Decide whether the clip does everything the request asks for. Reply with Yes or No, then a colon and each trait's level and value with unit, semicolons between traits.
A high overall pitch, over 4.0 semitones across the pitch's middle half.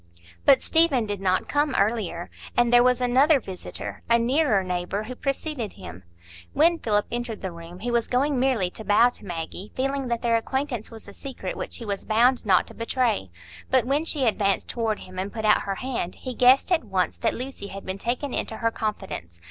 Yes: high, 230 Hz; average, 4.6 semitones